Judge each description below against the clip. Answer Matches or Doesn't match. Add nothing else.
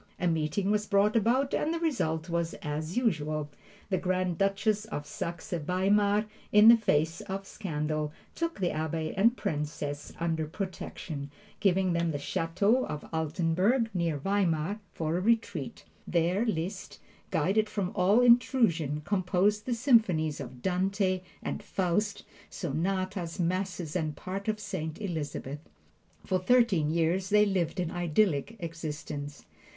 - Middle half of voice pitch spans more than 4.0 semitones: Matches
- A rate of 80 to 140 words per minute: Matches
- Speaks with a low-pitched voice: Doesn't match